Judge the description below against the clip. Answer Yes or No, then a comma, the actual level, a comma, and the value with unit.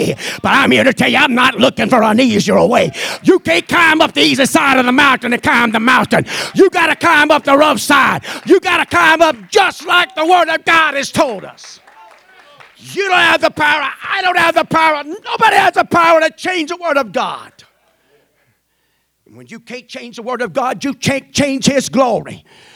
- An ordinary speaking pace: No, fast, 220 wpm